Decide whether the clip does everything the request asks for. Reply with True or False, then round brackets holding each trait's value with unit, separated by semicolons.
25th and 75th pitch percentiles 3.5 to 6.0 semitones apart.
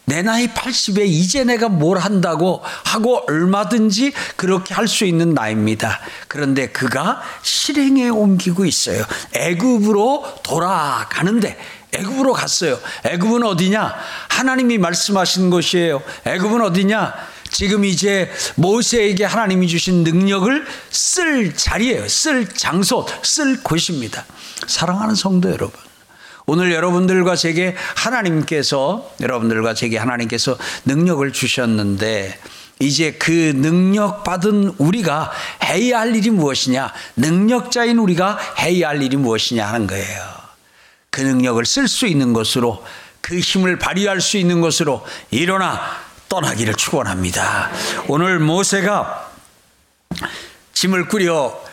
False (6.7 semitones)